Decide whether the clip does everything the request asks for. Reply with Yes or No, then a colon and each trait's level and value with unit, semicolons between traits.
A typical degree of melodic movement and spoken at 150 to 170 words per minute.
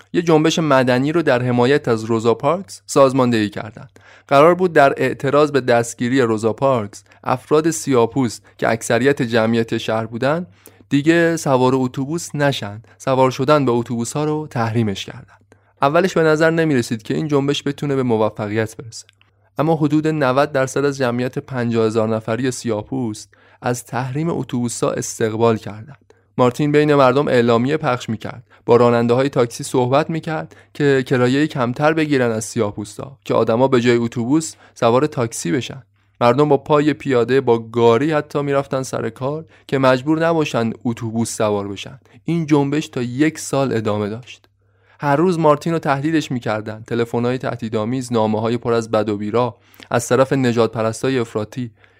Yes: average, 3.9 semitones; fast, 155 wpm